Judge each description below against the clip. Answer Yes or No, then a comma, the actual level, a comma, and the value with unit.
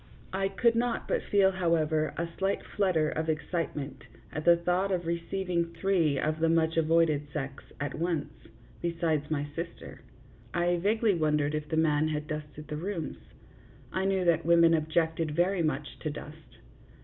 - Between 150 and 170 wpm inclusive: Yes, average, 160 wpm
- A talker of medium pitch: Yes, medium, 165 Hz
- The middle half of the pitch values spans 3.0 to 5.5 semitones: No, narrow, 2.5 semitones